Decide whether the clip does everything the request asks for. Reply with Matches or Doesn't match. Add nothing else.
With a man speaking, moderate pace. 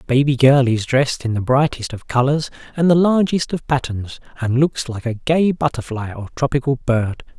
Matches